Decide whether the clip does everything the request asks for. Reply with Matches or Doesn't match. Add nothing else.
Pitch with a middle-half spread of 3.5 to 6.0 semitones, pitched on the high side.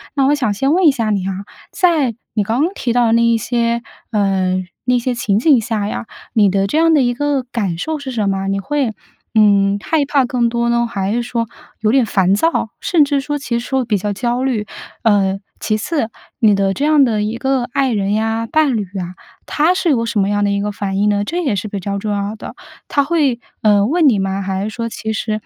Matches